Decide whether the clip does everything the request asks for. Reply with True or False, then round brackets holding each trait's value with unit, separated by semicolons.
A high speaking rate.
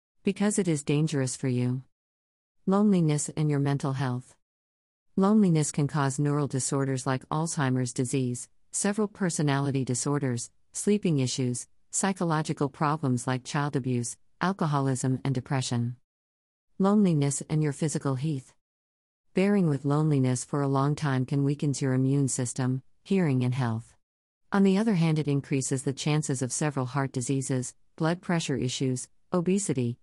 False (135 wpm)